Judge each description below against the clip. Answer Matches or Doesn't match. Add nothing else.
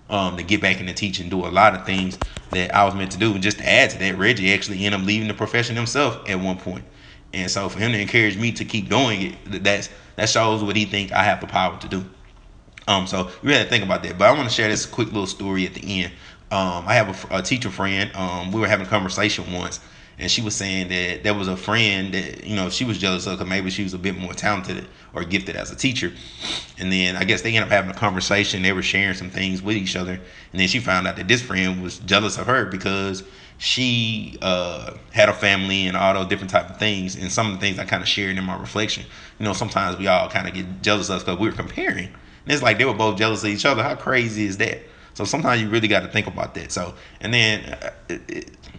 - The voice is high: Doesn't match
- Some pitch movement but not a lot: Doesn't match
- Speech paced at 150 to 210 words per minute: Doesn't match